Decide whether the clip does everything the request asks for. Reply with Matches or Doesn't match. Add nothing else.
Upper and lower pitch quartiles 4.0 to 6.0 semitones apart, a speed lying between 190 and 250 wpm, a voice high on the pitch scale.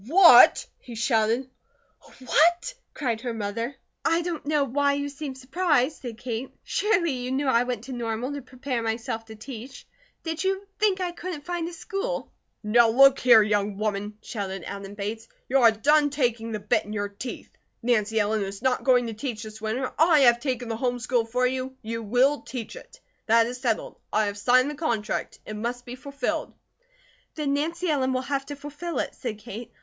Matches